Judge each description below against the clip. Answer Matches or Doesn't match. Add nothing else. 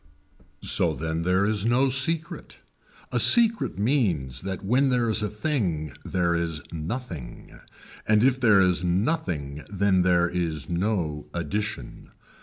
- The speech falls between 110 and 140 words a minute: Matches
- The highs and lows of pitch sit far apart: Matches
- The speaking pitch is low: Matches